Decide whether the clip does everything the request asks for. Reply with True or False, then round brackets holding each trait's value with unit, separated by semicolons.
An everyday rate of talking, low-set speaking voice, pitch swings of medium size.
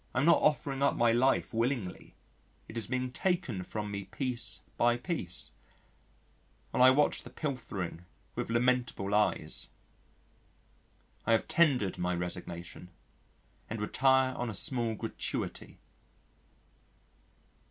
False (120 wpm; 120 Hz; 4.5 semitones)